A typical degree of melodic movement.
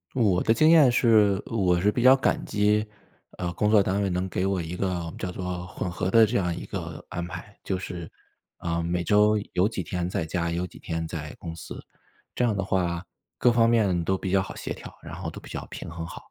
Yes: average, 3.2 semitones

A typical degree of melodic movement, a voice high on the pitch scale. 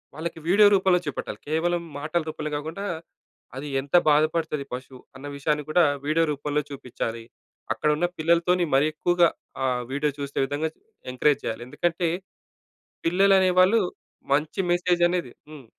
No: average, 3.3 semitones; medium, 155 Hz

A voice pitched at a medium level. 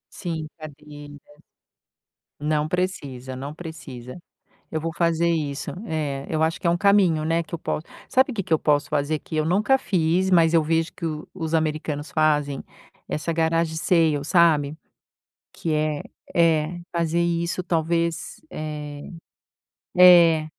Yes: medium, 160 Hz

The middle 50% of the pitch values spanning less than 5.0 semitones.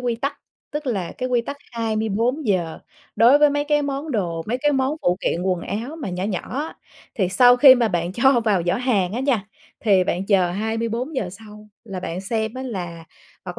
No: wide, 5.5 semitones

